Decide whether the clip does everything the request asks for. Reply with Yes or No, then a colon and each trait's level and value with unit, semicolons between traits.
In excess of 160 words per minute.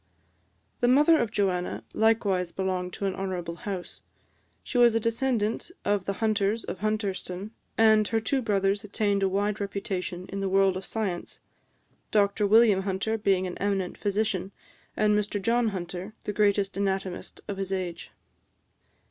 No: average, 155 wpm